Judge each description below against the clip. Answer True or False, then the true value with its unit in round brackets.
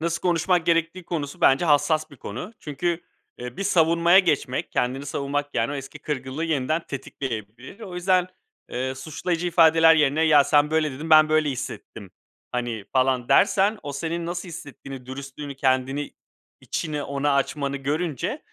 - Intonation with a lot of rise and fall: False (3.7 semitones)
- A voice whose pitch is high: False (150 Hz)